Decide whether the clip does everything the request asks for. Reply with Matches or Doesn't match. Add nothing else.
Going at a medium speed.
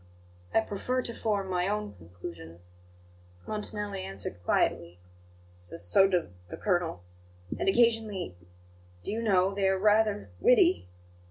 Doesn't match